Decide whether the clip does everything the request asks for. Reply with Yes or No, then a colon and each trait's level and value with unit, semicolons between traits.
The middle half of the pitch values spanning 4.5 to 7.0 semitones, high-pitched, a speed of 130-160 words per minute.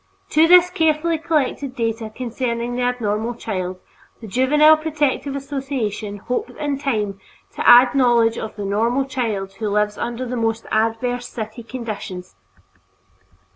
No: average, 4.0 semitones; high, 240 Hz; slow, 135 wpm